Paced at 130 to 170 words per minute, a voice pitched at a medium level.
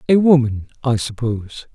Yes: average, 140 wpm; medium, 145 Hz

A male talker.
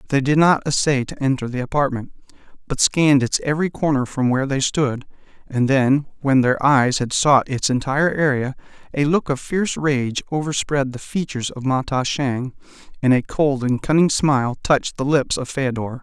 Yes: male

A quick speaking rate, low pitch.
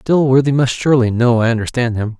No: average, 190 wpm; low, 125 Hz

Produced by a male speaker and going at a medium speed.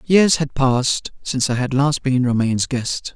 Yes: male; average, 190 wpm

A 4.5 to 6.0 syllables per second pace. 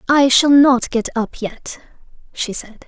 No: 3.9 syllables/s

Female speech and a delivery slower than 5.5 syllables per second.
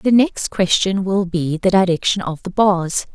Yes: female; 4.3 syllables/s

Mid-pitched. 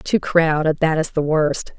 Yes: medium, 155 Hz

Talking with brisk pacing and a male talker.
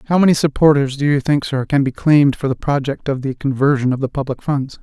Yes: fast, 250 wpm; male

